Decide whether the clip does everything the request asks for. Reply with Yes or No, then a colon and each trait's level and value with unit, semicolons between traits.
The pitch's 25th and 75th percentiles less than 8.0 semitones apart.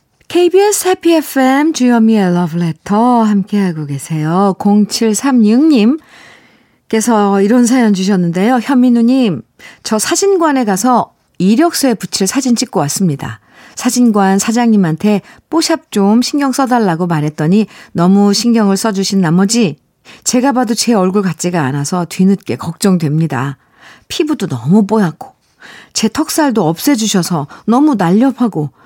Yes: wide, 5.5 semitones